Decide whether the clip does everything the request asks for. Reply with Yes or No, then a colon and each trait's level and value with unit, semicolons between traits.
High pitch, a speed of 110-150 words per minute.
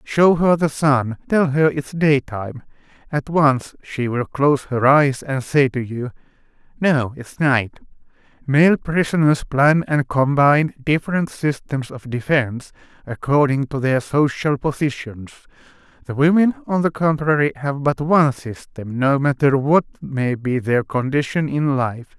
No: medium, 140 Hz; average, 145 wpm